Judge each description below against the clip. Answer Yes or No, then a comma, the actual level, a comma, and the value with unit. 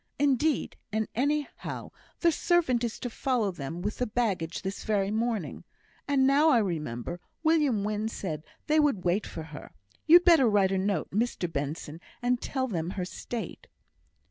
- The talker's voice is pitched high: Yes, high, 220 Hz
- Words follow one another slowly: No, average, 165 wpm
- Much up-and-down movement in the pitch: Yes, wide, 6.7 semitones